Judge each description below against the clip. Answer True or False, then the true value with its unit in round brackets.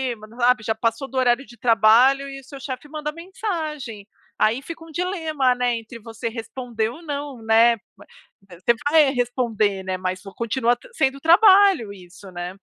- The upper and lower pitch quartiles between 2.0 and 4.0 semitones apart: False (4.6 semitones)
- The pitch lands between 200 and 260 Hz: True (245 Hz)